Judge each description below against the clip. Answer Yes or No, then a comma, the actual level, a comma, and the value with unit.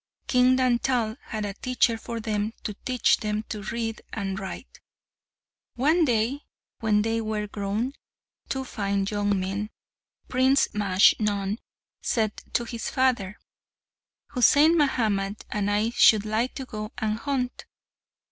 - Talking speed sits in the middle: No, slow, 130 wpm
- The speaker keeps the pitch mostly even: No, average, 3.3 semitones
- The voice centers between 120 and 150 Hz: No, high, 220 Hz